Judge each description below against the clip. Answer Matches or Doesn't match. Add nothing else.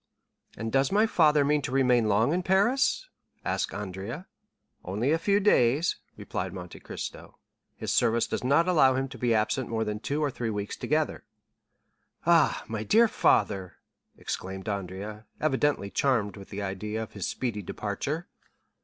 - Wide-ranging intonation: Matches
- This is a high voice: Doesn't match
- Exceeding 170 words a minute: Doesn't match